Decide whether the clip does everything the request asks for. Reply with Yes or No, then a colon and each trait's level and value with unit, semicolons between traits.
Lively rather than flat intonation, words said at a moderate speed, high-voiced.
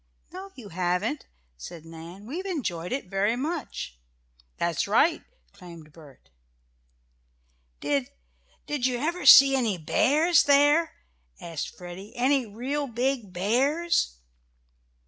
No: wide, 8.5 semitones; slow, 110 wpm; high, 230 Hz